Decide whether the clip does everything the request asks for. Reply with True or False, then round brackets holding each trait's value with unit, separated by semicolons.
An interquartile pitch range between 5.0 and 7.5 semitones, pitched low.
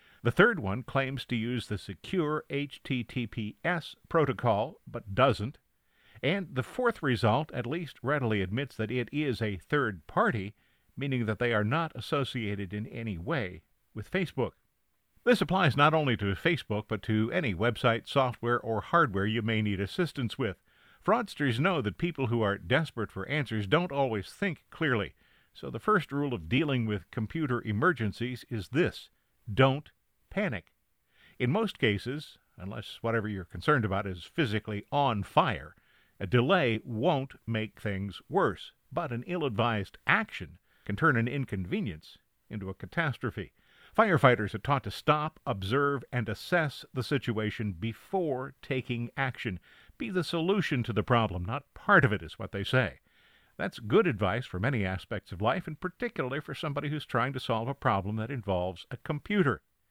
True (5.3 semitones; 120 Hz)